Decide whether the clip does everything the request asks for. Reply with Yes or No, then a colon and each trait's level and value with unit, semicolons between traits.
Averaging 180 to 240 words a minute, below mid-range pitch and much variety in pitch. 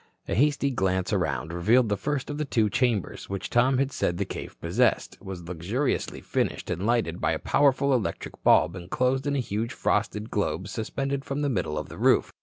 Yes: average, 200 wpm; low, 115 Hz; wide, 6.5 semitones